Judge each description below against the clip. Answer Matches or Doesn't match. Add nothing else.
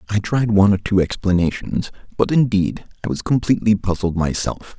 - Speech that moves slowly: Doesn't match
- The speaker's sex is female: Doesn't match